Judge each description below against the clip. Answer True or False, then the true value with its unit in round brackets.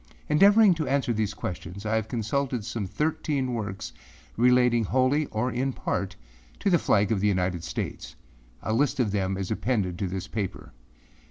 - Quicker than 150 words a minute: True (170 wpm)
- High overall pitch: False (110 Hz)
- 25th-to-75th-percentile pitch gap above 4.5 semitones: True (5.0 semitones)